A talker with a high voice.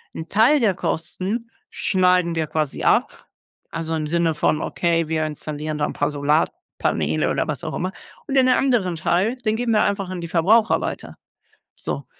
No: medium, 170 Hz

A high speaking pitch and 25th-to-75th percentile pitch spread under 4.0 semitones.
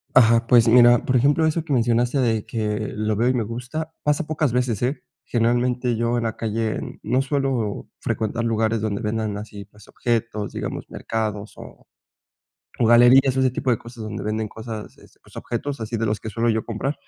No: low, 115 Hz; narrow, 2.4 semitones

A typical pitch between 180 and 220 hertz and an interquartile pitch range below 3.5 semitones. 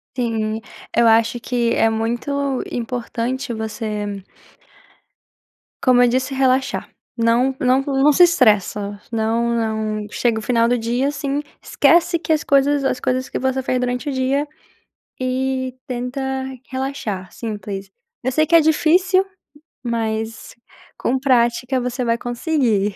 No: high, 245 Hz; average, 3.0 semitones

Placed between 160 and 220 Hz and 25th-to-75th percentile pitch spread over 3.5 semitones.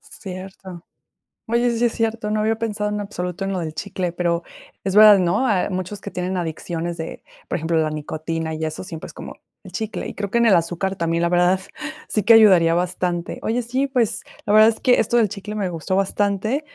Yes: high, 190 Hz; average, 3.9 semitones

